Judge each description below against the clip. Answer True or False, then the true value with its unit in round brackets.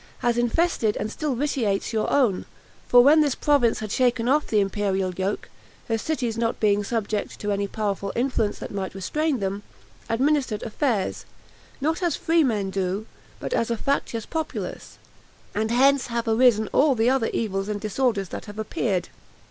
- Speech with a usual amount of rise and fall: True (4.5 semitones)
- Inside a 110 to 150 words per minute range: False (170 wpm)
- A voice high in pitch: True (225 Hz)